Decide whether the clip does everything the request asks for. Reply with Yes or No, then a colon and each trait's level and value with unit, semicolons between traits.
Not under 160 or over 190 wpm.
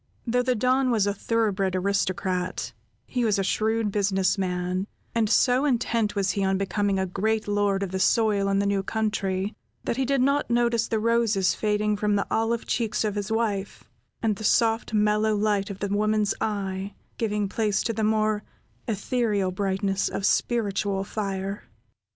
Yes: average, 175 wpm